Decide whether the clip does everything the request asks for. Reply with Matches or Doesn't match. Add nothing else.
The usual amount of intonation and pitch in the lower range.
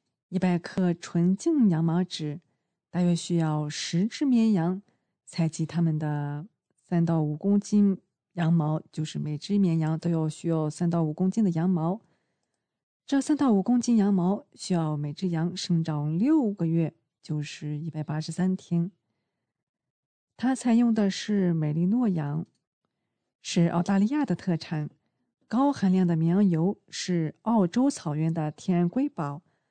Doesn't match